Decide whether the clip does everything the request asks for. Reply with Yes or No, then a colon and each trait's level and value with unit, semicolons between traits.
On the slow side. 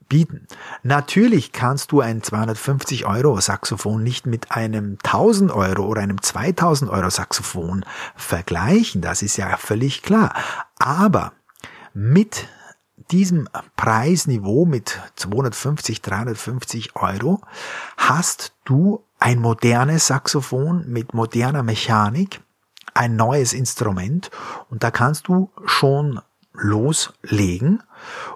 Yes: slow, 105 wpm